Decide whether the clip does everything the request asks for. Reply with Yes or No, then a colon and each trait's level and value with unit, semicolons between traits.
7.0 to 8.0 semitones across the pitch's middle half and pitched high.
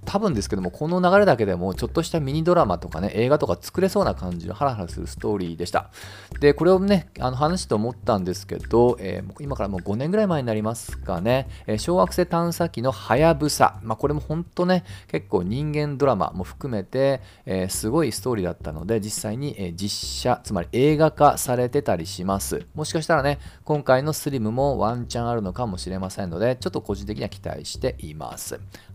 No: wide, 7.4 semitones; low, 120 Hz